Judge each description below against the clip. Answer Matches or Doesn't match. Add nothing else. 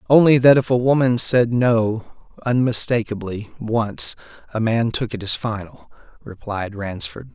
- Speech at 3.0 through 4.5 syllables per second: Matches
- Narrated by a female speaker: Doesn't match